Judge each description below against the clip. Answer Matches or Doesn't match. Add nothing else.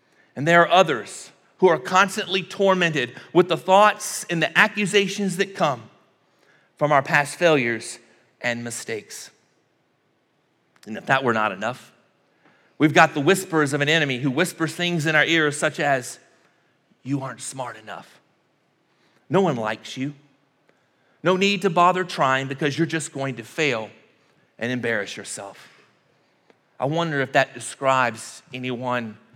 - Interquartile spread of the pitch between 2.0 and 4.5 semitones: Doesn't match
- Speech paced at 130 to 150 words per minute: Matches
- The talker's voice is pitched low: Doesn't match